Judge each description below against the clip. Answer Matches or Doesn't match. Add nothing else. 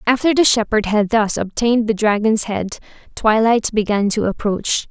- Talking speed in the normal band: Matches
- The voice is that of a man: Doesn't match